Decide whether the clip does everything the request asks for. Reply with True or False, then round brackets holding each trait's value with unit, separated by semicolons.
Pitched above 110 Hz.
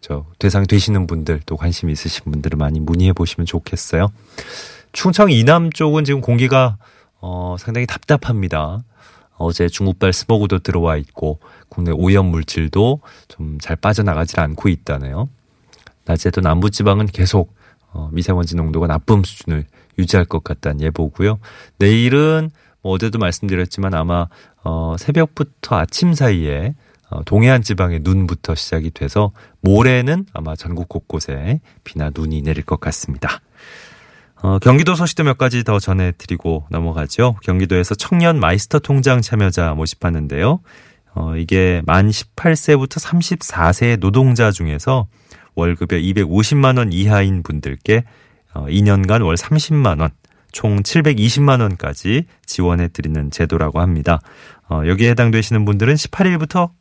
False (95 Hz)